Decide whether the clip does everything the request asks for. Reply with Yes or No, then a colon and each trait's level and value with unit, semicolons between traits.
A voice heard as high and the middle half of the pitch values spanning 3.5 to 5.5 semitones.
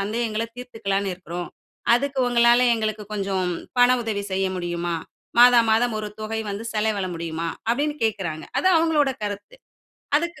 Yes: high, 215 Hz; average, 4.0 semitones